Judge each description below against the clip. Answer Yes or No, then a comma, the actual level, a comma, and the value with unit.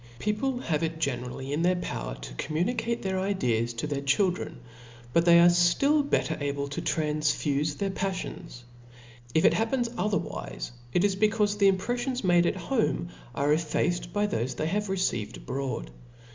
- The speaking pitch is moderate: Yes, medium, 175 Hz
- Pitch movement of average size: No, wide, 6.4 semitones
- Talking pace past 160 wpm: Yes, average, 170 wpm